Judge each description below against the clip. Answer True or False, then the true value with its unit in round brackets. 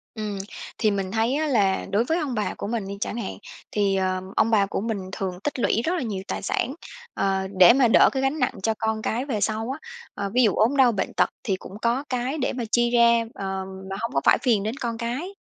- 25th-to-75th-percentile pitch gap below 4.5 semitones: True (4.0 semitones)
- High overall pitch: True (225 Hz)